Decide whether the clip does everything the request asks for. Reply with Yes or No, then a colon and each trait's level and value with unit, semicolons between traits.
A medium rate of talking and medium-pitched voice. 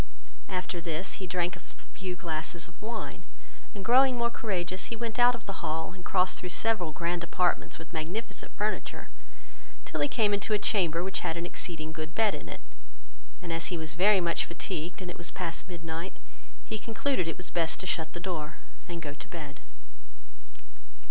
Yes: average, 190 wpm; medium, 180 Hz